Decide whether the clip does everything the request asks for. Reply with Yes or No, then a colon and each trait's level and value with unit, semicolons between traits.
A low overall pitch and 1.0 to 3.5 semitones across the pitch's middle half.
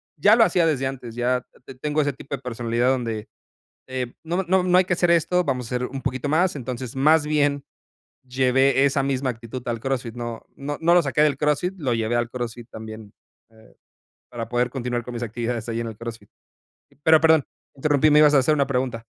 No: low, 130 Hz; average, 3.9 semitones